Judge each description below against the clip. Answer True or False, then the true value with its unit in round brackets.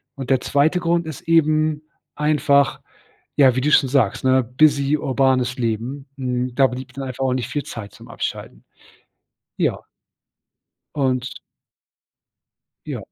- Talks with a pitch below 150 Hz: True (135 Hz)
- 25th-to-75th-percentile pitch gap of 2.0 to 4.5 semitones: True (2.7 semitones)